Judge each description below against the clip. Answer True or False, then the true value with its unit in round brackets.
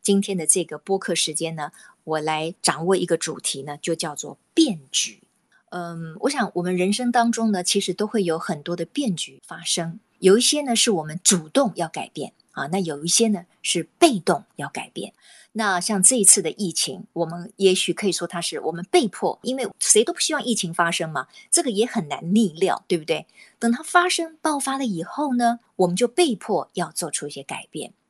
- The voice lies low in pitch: False (190 Hz)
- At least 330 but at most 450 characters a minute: False (290 characters per minute)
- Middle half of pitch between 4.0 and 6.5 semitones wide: True (5.5 semitones)